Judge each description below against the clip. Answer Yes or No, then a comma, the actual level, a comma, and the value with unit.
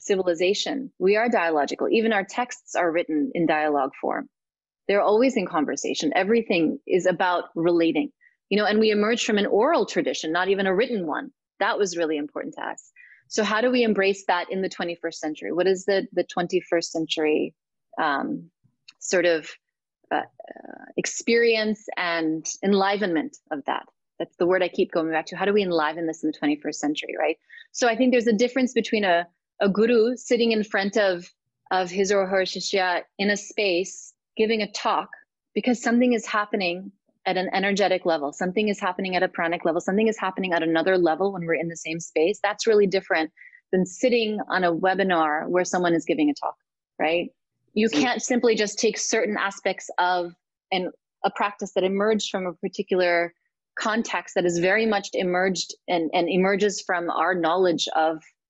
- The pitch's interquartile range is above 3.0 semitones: Yes, average, 3.8 semitones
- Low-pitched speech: No, high, 190 Hz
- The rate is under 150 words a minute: No, average, 185 wpm